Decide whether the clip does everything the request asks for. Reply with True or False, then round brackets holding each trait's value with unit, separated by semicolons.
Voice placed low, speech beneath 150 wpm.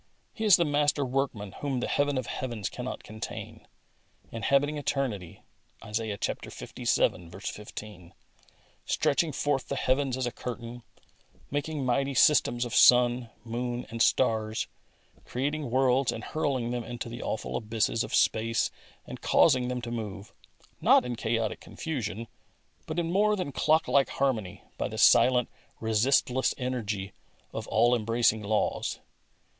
True (125 Hz; 140 wpm)